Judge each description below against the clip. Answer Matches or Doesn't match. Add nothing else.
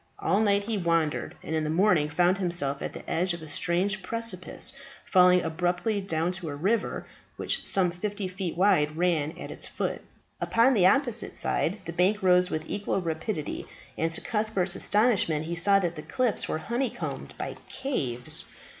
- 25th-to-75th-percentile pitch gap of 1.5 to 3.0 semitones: Doesn't match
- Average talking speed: Matches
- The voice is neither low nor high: Matches